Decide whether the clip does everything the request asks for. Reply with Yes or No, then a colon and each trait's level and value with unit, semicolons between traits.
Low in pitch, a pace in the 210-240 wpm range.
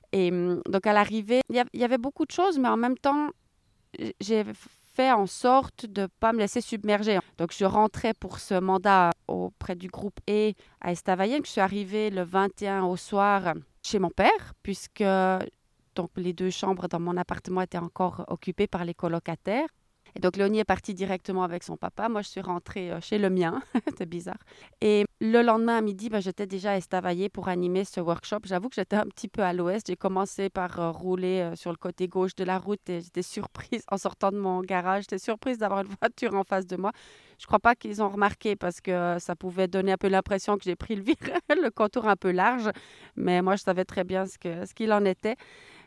No: high, 195 Hz; average, 215 wpm